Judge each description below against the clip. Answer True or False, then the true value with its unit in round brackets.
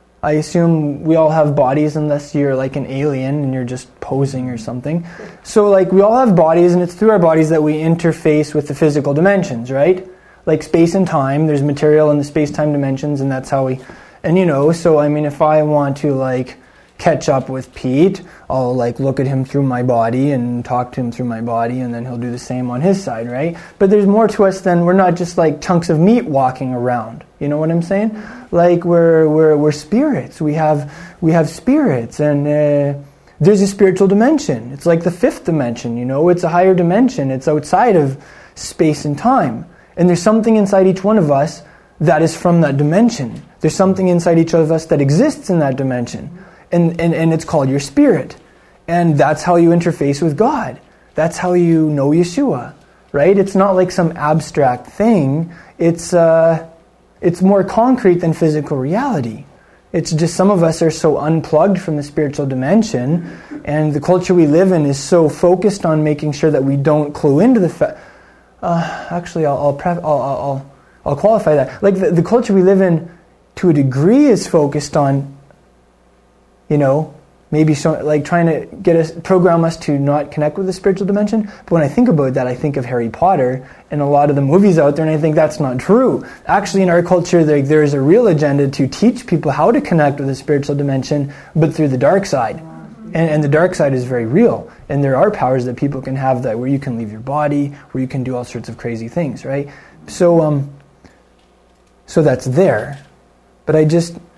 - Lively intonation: False (3.9 semitones)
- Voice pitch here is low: False (155 Hz)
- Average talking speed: False (210 wpm)